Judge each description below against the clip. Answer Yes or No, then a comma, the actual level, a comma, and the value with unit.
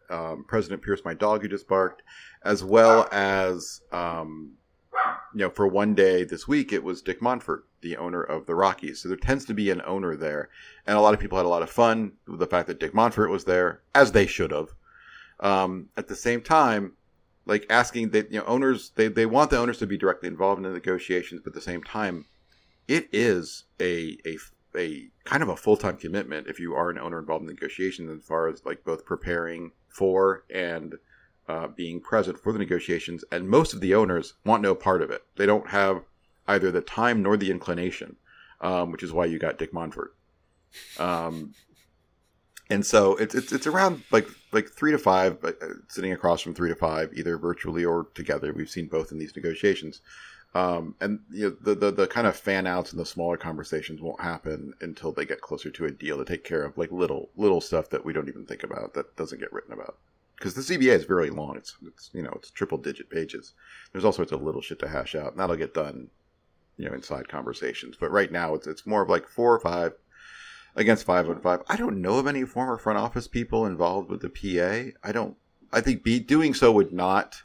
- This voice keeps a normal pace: No, fast, 220 wpm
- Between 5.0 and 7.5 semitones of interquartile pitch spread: No, average, 3.6 semitones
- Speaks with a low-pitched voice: Yes, very low, 95 Hz